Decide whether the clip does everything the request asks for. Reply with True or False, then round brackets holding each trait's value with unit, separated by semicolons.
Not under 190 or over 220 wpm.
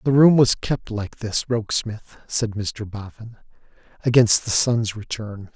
False (150 wpm)